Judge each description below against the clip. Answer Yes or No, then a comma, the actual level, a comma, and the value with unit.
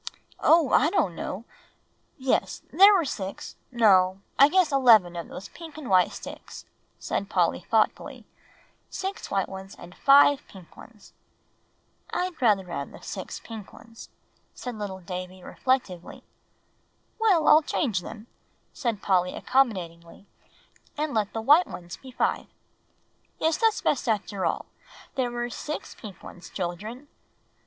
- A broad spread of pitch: Yes, wide, 6.8 semitones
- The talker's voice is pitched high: Yes, high, 220 Hz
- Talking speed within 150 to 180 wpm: No, average, 140 wpm